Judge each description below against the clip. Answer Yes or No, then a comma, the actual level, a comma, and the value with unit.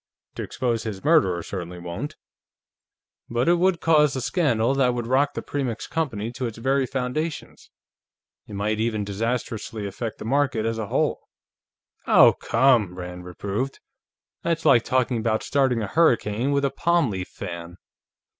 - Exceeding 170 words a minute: No, average, 155 wpm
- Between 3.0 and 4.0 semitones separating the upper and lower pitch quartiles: No, average, 4.8 semitones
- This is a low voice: Yes, low, 120 Hz